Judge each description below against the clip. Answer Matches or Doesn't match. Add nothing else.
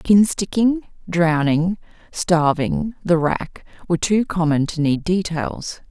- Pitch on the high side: Doesn't match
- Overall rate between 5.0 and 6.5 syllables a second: Doesn't match